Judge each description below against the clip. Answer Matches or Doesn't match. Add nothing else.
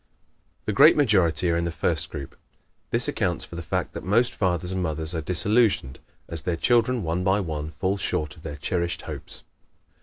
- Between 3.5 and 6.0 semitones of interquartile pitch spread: Doesn't match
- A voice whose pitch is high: Doesn't match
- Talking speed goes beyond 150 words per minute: Matches